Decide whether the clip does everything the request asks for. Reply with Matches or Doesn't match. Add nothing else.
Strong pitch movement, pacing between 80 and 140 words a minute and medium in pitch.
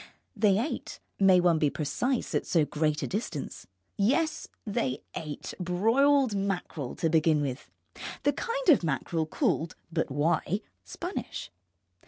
Matches